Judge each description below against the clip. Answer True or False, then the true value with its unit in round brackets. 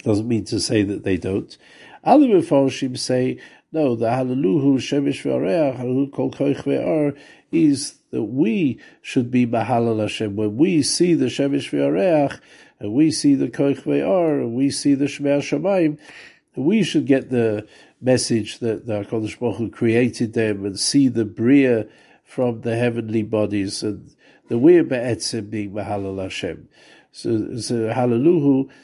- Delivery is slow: False (145 wpm)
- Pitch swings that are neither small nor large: True (4.2 semitones)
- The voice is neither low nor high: False (120 Hz)